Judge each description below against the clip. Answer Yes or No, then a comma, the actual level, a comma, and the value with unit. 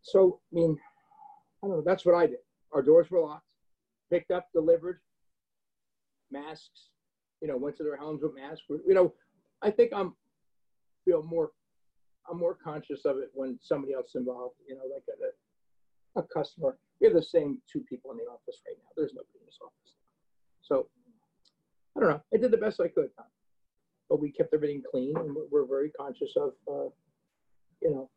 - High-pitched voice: Yes, high, 210 Hz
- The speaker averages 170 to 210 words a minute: Yes, average, 195 wpm